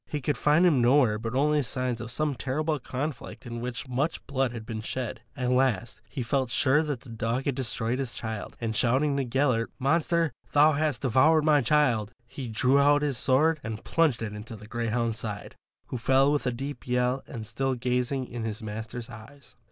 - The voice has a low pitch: Yes, low, 125 Hz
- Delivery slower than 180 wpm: No, average, 200 wpm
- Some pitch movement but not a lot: Yes, average, 3.6 semitones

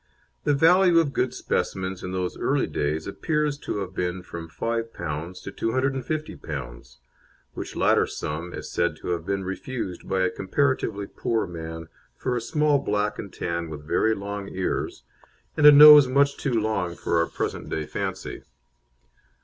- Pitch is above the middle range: No, low, 100 Hz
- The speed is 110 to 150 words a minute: No, average, 160 wpm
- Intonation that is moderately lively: No, wide, 7.4 semitones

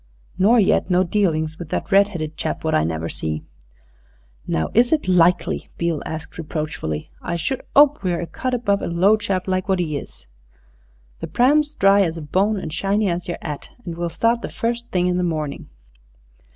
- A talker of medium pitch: Yes, medium, 180 Hz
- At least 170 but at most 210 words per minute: Yes, average, 190 wpm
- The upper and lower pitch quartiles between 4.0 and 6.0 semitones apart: Yes, average, 4.3 semitones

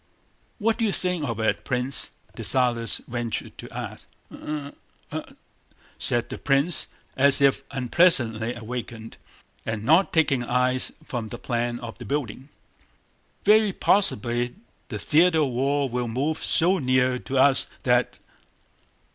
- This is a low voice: Yes, low, 130 Hz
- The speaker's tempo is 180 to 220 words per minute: No, average, 140 wpm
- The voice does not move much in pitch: No, average, 4.0 semitones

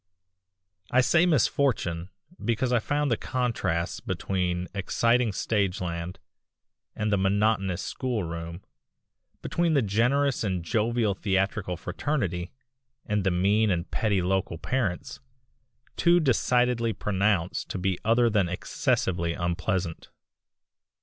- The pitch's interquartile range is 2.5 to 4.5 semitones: No, average, 5.0 semitones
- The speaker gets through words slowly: Yes, slow, 110 wpm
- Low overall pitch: Yes, low, 100 Hz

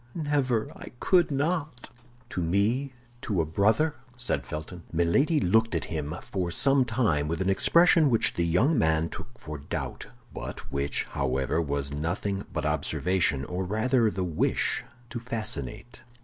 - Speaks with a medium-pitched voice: No, low, 100 Hz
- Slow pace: No, average, 150 wpm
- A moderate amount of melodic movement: No, wide, 7.7 semitones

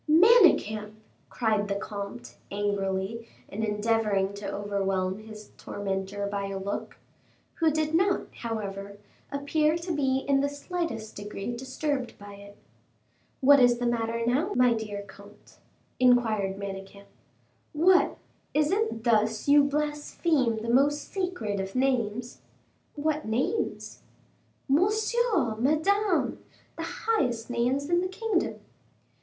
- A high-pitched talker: Yes, high, 235 Hz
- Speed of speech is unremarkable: No, slow, 125 wpm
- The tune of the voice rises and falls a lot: Yes, wide, 6.7 semitones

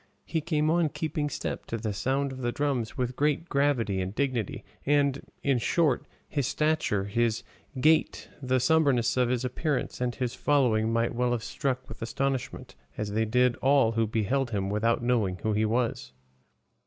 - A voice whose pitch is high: No, low, 125 Hz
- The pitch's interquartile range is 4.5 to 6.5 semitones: No, average, 3.9 semitones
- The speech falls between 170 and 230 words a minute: Yes, average, 175 wpm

